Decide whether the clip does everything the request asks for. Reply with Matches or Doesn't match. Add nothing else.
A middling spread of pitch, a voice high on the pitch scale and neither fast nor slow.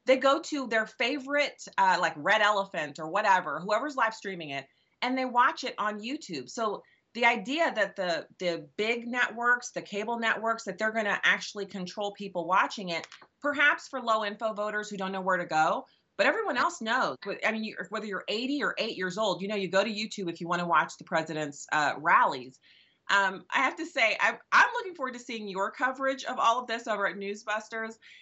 Doesn't match